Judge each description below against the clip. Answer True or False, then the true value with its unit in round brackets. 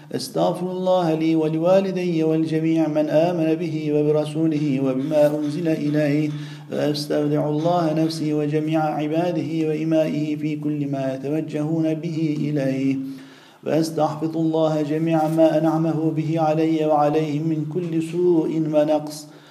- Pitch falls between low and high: True (155 Hz)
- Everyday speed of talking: True (110 wpm)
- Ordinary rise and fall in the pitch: False (1.1 semitones)